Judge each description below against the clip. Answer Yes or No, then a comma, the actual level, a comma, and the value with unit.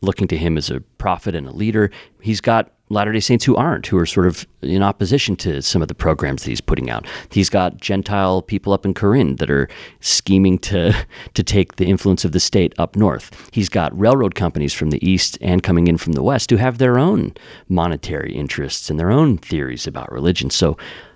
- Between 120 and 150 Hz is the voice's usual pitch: No, very low, 95 Hz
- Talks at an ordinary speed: No, fast, 215 wpm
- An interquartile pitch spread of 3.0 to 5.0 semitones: Yes, average, 3.9 semitones